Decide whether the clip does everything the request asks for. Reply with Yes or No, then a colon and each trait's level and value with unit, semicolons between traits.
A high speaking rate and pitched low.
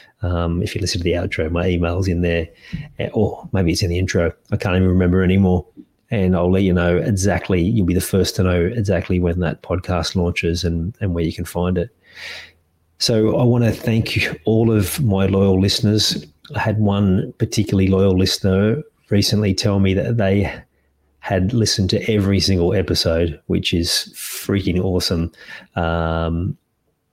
No: average, 175 wpm; very low, 95 Hz